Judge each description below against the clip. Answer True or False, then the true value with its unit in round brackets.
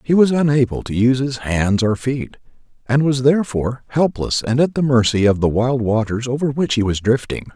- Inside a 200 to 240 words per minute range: True (205 wpm)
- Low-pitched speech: True (125 Hz)